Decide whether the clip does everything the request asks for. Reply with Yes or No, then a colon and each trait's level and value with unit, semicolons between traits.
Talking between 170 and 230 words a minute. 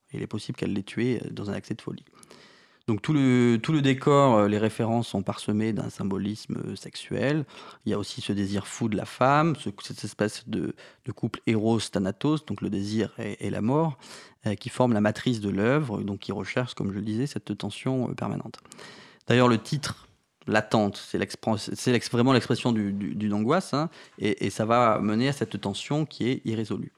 Yes: average, 205 wpm